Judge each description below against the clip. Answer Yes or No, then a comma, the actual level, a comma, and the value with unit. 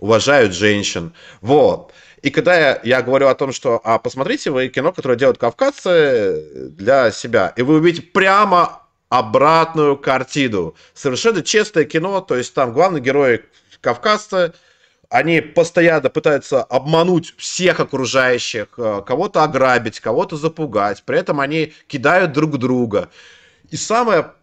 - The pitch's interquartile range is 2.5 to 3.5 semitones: No, average, 5.2 semitones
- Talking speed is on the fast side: No, average, 130 wpm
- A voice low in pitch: No, medium, 155 Hz